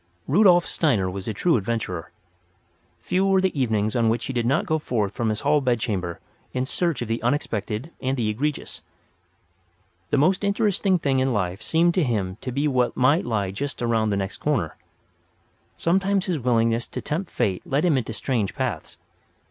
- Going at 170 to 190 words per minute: Yes, average, 180 wpm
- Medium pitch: No, low, 125 Hz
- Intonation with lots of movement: Yes, wide, 6.4 semitones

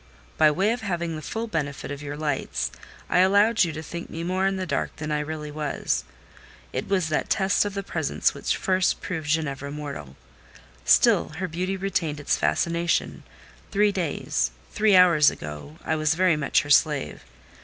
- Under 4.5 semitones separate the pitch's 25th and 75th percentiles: Yes, average, 4.1 semitones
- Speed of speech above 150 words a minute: Yes, average, 175 wpm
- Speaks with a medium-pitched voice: Yes, medium, 160 Hz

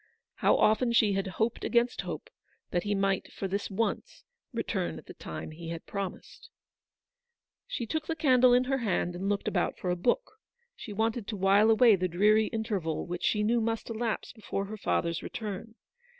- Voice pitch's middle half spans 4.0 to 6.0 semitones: No, average, 3.3 semitones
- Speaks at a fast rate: No, average, 185 wpm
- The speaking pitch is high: Yes, high, 210 Hz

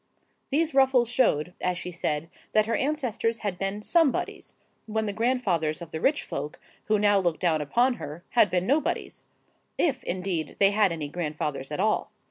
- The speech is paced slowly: No, average, 170 wpm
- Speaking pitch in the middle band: No, high, 200 Hz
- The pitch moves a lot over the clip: Yes, wide, 6.4 semitones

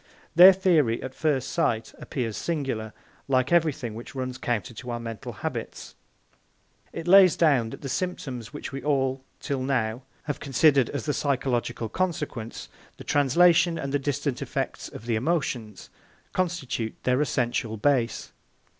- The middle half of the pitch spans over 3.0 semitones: Yes, average, 4.3 semitones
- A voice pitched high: No, low, 135 Hz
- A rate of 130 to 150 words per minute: Yes, average, 145 wpm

